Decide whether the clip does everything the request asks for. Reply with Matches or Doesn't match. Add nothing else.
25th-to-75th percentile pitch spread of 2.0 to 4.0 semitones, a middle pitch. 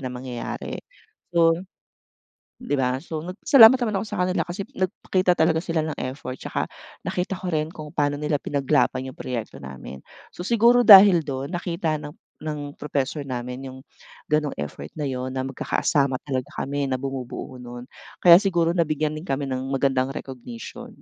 Doesn't match